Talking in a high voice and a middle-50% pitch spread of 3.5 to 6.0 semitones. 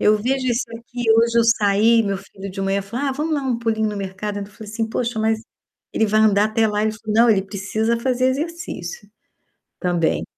No: high, 220 Hz; narrow, 2.6 semitones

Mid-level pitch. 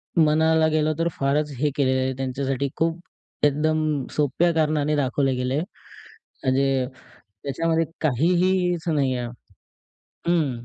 Yes: medium, 150 Hz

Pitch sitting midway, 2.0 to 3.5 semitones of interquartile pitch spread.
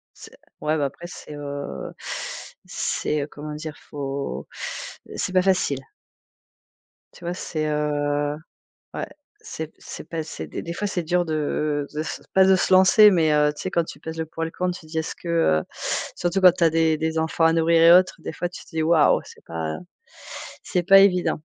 Yes: medium, 160 Hz; average, 2.9 semitones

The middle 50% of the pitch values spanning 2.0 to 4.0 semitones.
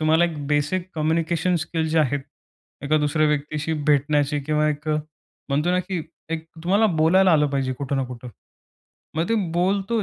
Yes: average, 2.8 semitones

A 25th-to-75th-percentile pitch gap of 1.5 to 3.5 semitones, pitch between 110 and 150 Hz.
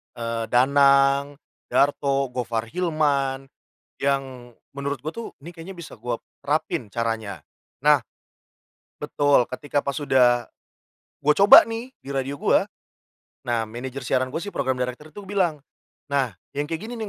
Yes: average, 3.2 semitones; medium, 140 Hz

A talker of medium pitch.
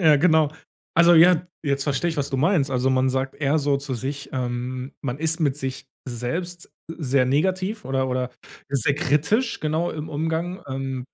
Yes: medium, 145 Hz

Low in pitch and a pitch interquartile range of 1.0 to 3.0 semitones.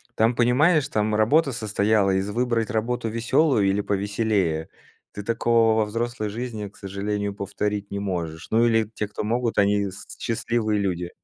Yes: low, 110 Hz; narrow, 2.6 semitones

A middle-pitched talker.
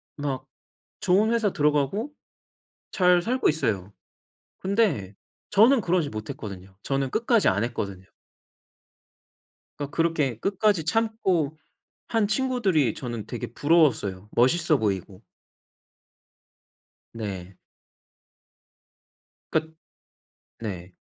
Yes: medium, 150 Hz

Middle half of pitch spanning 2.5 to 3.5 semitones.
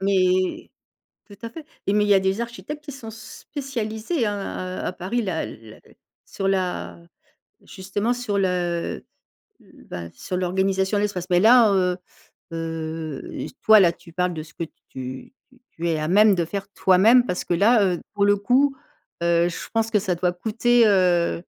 No: average, 3.9 semitones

